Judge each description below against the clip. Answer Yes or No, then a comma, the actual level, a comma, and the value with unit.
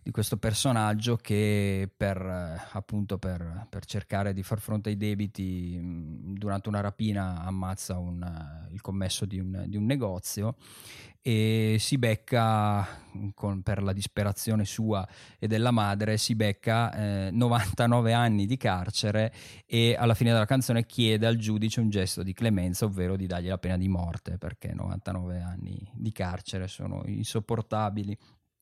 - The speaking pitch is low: Yes, low, 105 Hz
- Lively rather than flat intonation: No, average, 2.8 semitones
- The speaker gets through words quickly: No, average, 155 wpm